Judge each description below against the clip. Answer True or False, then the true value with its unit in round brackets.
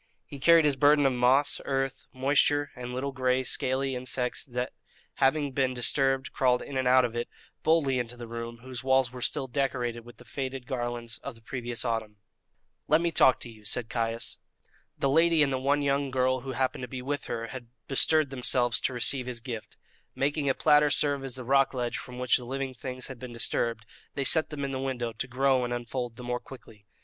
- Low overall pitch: True (130 Hz)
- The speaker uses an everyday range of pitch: False (2.1 semitones)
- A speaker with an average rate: False (215 wpm)